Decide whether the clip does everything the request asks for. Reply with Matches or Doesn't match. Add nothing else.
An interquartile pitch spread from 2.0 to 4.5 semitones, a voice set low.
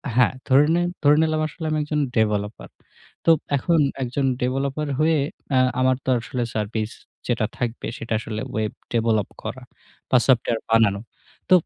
Doesn't match